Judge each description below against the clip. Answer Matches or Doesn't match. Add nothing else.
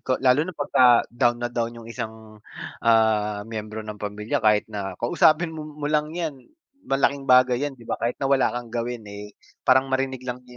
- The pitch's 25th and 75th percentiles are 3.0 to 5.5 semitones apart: Matches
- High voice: Doesn't match